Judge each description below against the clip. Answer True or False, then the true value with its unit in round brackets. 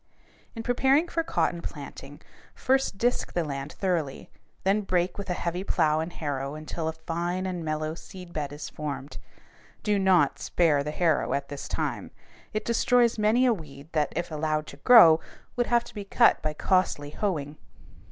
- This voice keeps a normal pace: True (175 wpm)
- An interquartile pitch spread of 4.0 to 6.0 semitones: True (5.2 semitones)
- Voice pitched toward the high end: False (170 Hz)